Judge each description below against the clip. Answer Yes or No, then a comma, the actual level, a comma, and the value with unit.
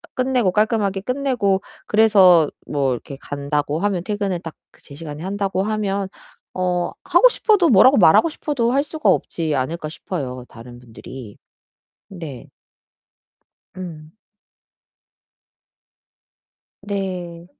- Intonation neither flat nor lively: No, wide, 5.8 semitones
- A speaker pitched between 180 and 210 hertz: Yes, medium, 185 Hz